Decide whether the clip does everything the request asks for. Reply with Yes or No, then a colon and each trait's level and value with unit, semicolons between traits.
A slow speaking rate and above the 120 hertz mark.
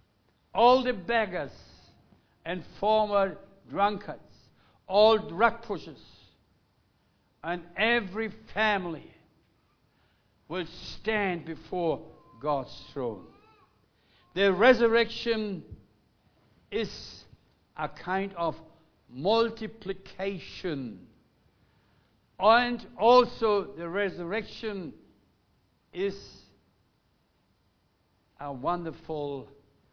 Yes: slow, 60 wpm; high, 190 Hz